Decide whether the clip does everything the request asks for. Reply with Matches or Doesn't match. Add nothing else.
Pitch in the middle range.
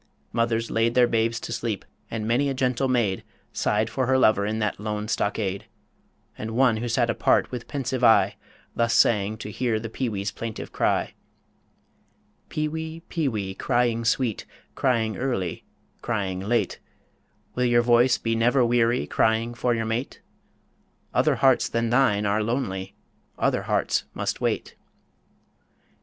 Doesn't match